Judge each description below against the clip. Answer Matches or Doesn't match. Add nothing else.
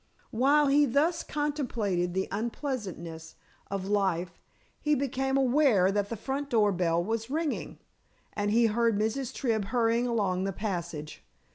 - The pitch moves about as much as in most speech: Doesn't match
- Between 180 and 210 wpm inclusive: Doesn't match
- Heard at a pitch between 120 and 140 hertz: Doesn't match